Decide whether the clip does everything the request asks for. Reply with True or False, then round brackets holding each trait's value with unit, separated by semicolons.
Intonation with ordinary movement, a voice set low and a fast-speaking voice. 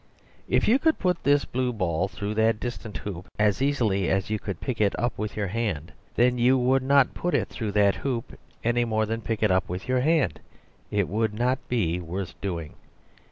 True (4.2 semitones; 110 Hz; 210 wpm)